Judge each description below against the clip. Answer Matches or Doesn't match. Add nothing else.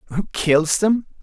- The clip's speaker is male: Matches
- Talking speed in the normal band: Matches